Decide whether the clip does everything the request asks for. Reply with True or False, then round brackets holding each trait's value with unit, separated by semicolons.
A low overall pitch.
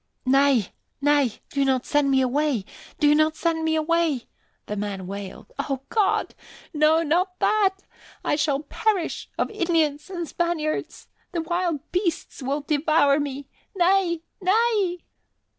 False (310 Hz)